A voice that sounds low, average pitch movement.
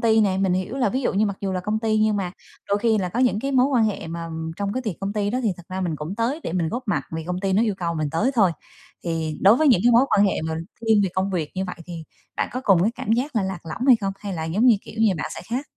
No: high, 200 Hz; average, 4.1 semitones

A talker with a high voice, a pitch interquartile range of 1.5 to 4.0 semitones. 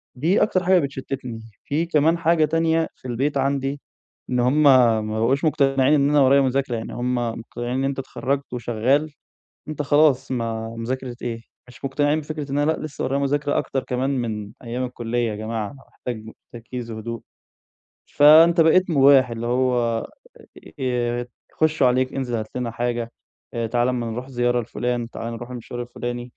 No: low, 130 Hz; average, 3.0 semitones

